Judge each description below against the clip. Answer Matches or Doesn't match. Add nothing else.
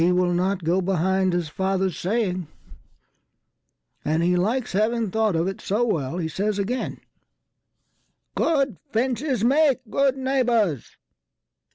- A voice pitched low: Doesn't match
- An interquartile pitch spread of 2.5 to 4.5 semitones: Doesn't match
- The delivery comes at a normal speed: Doesn't match